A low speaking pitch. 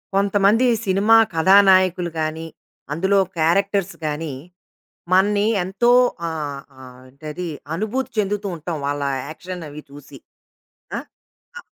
No: medium, 185 Hz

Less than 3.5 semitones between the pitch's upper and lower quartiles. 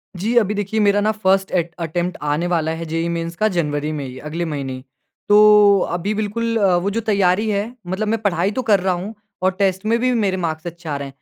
No: average, 3.9 semitones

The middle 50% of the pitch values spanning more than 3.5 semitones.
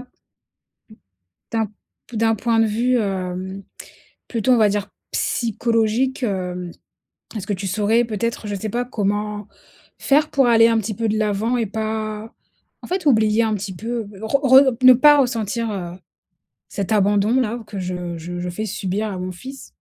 No: average, 2.9 semitones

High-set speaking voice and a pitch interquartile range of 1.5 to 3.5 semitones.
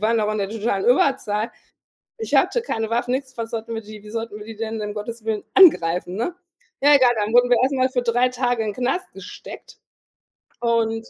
Yes: high, 230 Hz; narrow, 2.6 semitones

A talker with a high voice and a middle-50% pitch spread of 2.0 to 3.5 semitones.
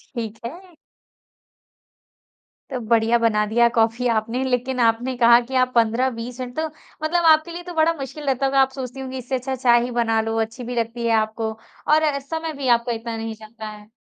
Yes: high, 245 Hz; average, 2.9 semitones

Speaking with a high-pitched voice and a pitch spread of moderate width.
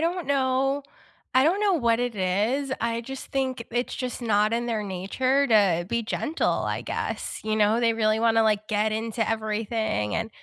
Yes: high, 230 Hz; average, 3.3 semitones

